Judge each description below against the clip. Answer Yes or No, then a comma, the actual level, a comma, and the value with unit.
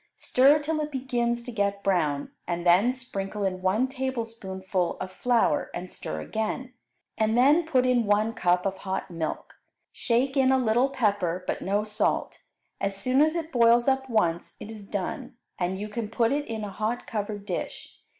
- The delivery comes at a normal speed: Yes, average, 180 wpm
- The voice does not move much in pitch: No, average, 4.8 semitones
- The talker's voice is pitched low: No, high, 220 Hz